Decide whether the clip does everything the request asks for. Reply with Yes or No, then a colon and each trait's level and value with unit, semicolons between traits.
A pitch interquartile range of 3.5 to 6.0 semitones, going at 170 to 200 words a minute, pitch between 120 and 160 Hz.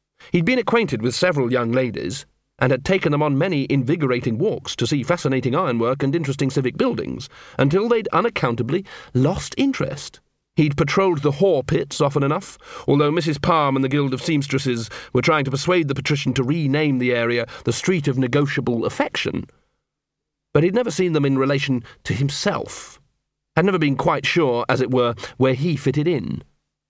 Yes: average, 4.1 semitones; average, 175 wpm; medium, 140 Hz